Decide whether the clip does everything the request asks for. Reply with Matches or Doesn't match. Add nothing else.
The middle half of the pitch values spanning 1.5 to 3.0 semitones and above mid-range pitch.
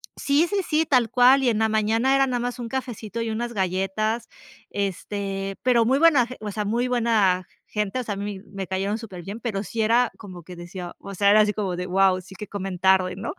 Doesn't match